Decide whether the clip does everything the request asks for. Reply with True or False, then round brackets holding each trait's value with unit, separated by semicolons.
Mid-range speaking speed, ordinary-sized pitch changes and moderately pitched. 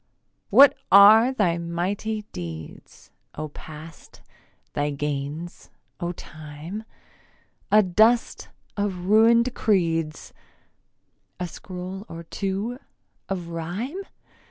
False (90 wpm; 4.7 semitones; 180 Hz)